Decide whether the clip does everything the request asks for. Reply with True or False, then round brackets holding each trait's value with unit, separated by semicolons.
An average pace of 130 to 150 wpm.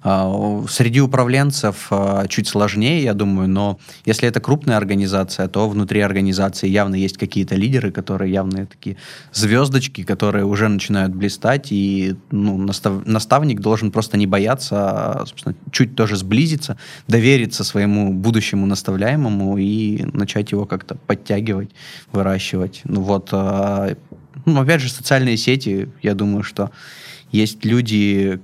True (135 wpm)